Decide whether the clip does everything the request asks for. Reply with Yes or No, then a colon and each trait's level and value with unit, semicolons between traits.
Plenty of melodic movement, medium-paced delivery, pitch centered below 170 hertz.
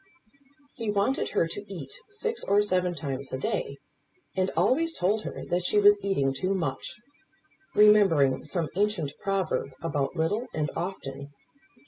No: wide, 5.7 semitones; average, 145 wpm; medium, 185 Hz